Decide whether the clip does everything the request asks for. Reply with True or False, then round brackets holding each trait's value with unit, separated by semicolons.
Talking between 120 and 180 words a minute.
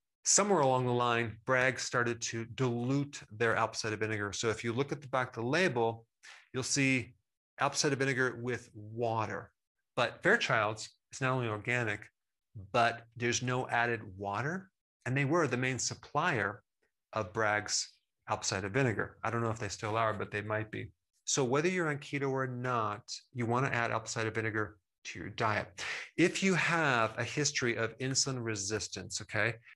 True (175 wpm)